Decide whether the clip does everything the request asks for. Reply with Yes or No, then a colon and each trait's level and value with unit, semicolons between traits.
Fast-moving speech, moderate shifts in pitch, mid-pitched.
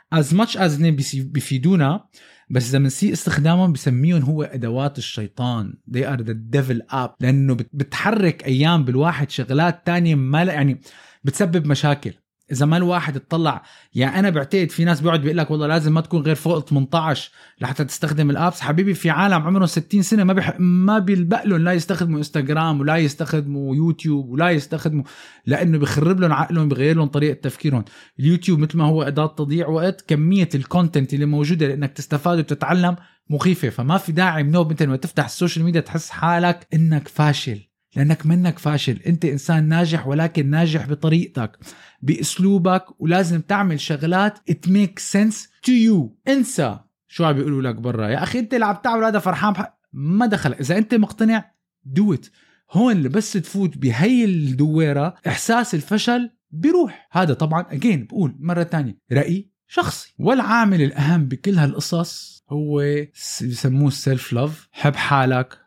Yes: fast, 155 wpm; average, 4.1 semitones; medium, 160 Hz